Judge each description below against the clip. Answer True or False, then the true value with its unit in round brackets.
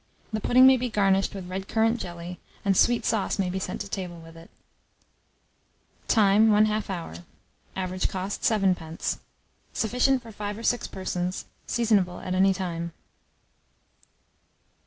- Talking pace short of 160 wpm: True (140 wpm)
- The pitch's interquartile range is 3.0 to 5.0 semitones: True (3.3 semitones)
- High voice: True (195 Hz)